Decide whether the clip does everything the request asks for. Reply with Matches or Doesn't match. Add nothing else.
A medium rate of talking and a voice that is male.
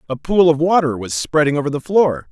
Doesn't match